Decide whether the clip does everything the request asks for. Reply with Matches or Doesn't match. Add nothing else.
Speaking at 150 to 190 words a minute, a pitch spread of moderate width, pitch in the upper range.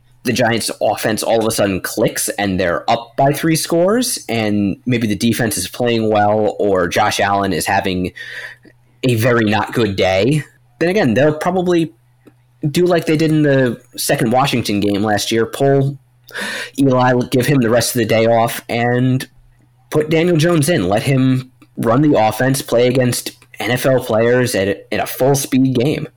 Doesn't match